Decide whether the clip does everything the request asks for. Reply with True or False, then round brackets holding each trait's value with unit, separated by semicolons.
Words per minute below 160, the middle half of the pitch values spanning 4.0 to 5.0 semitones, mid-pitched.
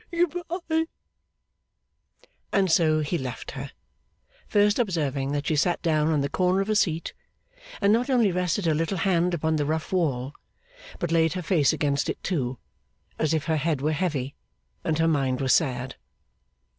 False (170 wpm; 4.3 semitones; 160 Hz)